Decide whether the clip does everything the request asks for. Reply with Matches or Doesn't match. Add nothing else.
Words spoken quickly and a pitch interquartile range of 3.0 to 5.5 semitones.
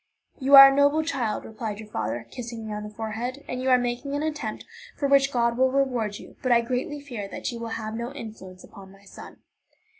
Matches